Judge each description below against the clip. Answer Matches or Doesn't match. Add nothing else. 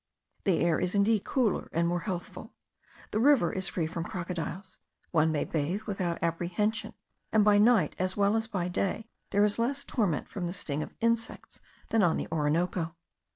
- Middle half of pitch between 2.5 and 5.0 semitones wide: Matches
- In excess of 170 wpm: Matches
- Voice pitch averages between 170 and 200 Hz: Matches